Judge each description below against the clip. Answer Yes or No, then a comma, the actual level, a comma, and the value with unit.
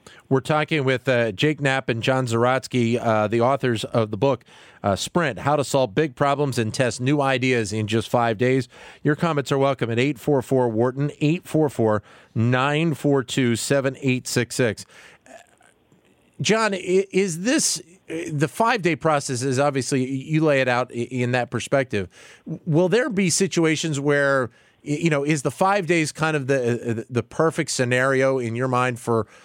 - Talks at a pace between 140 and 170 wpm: Yes, average, 155 wpm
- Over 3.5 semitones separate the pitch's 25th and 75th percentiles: Yes, average, 3.9 semitones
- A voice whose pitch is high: No, low, 135 Hz